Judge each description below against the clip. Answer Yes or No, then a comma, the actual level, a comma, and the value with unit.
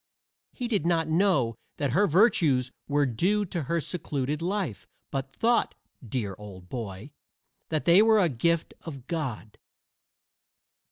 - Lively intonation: Yes, wide, 6.0 semitones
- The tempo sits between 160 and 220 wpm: No, slow, 135 wpm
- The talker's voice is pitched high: No, medium, 155 Hz